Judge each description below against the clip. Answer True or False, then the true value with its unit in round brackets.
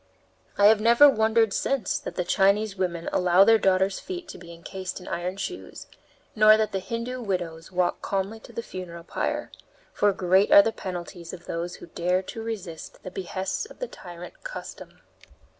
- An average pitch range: True (3.7 semitones)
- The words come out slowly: False (175 wpm)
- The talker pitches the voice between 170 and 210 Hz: True (190 Hz)